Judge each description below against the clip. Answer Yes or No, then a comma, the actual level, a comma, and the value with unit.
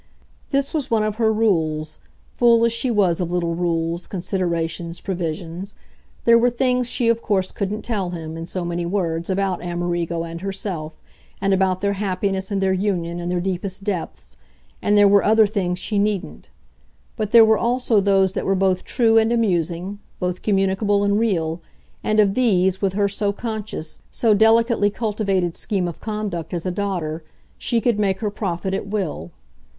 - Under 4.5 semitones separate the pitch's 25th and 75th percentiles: Yes, average, 3.5 semitones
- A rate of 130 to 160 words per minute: No, average, 175 wpm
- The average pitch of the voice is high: Yes, high, 195 Hz